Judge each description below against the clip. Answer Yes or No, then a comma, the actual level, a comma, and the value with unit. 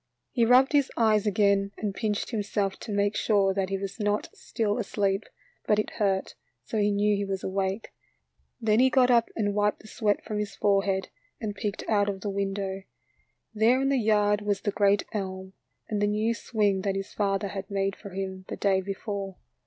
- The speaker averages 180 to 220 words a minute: Yes, average, 200 wpm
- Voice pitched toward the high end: Yes, high, 205 Hz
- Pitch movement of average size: No, narrow, 1.5 semitones